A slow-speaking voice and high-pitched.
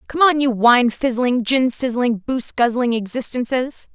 Yes: slow, 105 wpm; high, 245 Hz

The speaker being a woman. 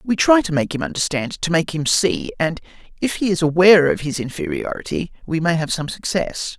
No: male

